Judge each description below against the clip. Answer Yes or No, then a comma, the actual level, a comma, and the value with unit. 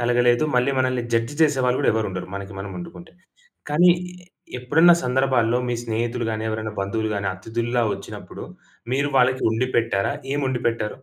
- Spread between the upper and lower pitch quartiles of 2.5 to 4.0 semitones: Yes, average, 2.8 semitones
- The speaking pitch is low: Yes, low, 120 Hz